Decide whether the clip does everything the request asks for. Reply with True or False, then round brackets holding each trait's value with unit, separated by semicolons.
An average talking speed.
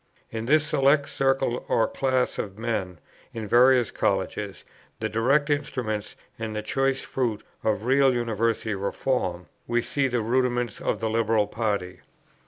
True (145 wpm)